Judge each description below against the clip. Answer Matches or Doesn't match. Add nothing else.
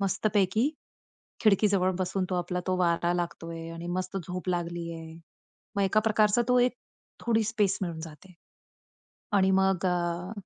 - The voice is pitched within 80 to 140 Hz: Doesn't match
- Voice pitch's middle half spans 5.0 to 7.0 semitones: Doesn't match